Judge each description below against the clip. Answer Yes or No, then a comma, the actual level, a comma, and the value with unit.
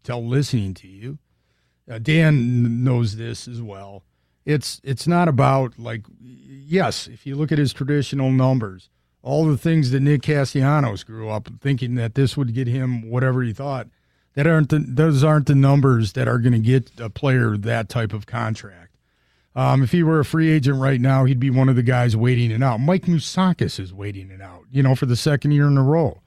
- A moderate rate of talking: No, fast, 210 wpm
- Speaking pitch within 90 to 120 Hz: No, low, 130 Hz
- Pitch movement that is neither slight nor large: Yes, average, 3.7 semitones